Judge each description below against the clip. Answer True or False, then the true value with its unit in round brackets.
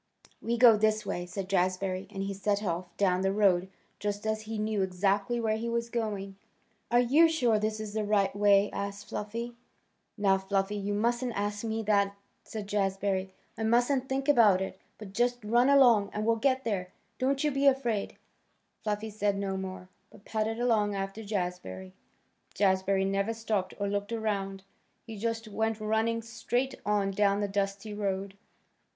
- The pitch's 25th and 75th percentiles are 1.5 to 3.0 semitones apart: True (2.5 semitones)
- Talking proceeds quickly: False (175 wpm)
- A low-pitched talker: False (210 Hz)